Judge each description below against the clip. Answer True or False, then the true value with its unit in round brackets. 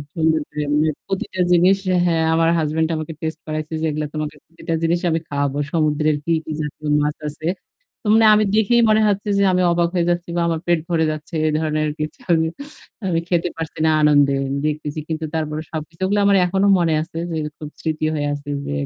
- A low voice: False (160 Hz)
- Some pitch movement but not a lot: False (2.0 semitones)